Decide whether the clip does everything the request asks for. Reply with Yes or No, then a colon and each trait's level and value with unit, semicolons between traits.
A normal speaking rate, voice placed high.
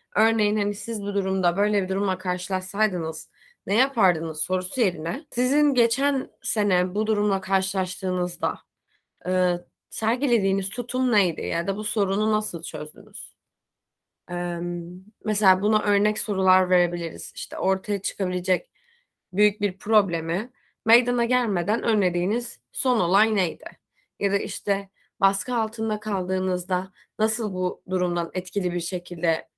Yes: average, 120 wpm; high, 195 Hz